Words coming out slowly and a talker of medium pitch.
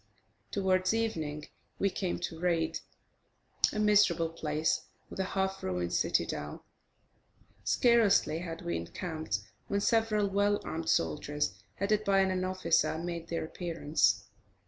Yes: slow, 125 wpm; medium, 175 Hz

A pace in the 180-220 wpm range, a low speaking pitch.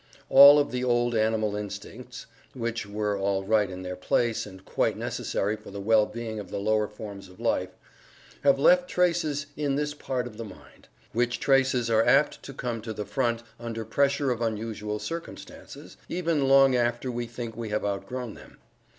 Yes: average, 185 wpm; low, 115 Hz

